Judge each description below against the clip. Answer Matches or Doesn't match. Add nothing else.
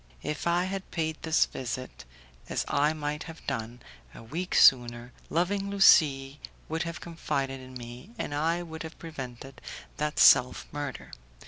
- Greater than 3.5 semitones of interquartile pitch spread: Matches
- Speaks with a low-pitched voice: Doesn't match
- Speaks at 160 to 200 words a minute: Doesn't match